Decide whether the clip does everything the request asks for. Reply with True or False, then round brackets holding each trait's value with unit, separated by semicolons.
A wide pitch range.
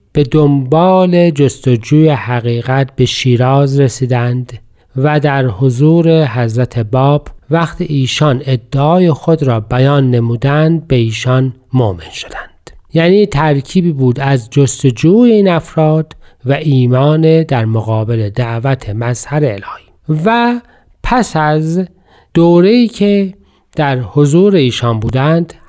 False (4.3 semitones)